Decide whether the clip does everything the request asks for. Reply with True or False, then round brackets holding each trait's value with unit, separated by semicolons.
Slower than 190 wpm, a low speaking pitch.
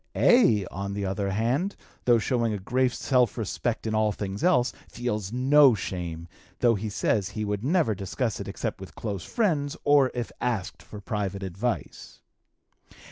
True (165 wpm; 110 Hz)